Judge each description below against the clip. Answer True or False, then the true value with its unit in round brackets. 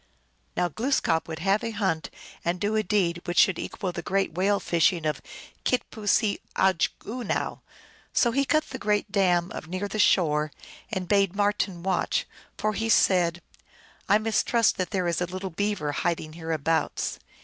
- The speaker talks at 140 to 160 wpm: False (170 wpm)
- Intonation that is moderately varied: True (3.5 semitones)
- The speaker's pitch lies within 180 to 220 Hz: True (190 Hz)